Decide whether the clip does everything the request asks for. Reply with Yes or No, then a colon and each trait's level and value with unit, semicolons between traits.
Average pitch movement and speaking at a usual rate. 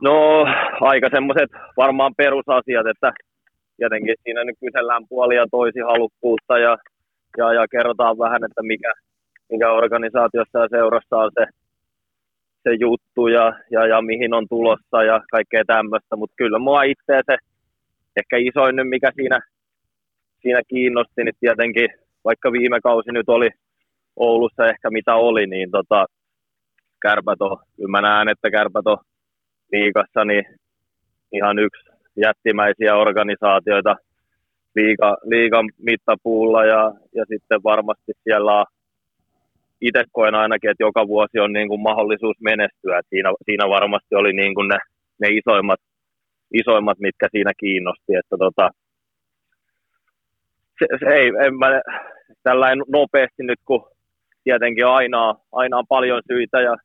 No: narrow, 2.2 semitones; average, 130 wpm